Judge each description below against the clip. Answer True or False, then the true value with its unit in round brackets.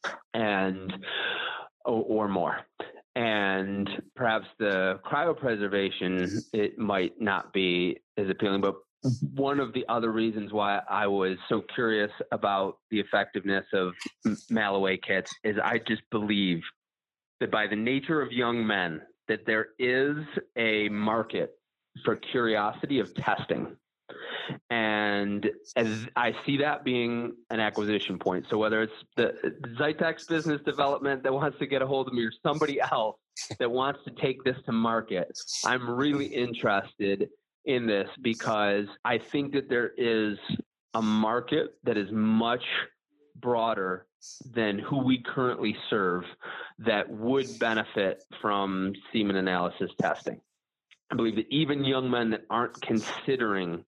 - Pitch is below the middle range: True (110 Hz)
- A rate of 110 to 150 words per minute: True (135 wpm)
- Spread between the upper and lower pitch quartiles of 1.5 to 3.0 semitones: False (4.5 semitones)